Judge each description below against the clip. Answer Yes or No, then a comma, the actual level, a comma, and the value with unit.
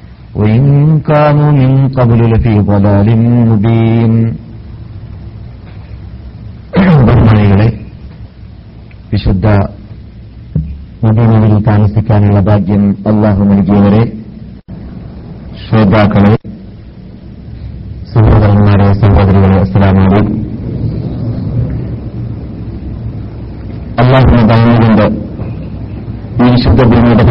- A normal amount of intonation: No, narrow, 1.9 semitones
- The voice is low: Yes, low, 110 Hz